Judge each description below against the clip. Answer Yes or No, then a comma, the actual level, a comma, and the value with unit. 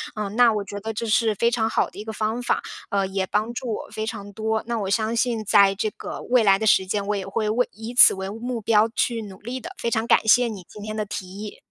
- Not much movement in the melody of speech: Yes, narrow, 2.2 semitones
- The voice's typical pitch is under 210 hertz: No, high, 215 Hz